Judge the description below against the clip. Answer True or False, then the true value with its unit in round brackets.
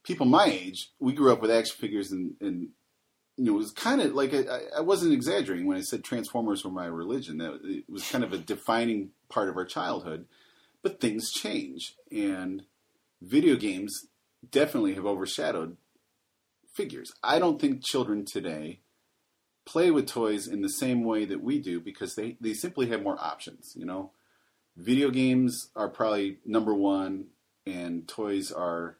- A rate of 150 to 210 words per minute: True (170 wpm)